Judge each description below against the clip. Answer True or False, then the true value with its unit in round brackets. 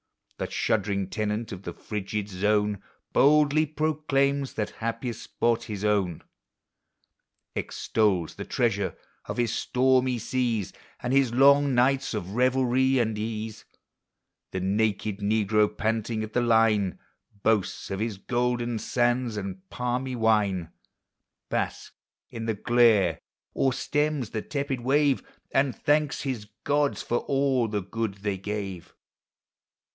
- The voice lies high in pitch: False (115 Hz)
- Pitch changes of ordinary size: True (3.8 semitones)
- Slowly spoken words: True (125 wpm)